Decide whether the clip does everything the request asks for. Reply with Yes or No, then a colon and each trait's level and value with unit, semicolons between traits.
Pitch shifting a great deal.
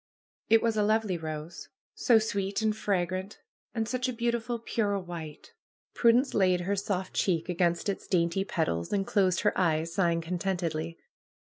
No: average, 4.1 semitones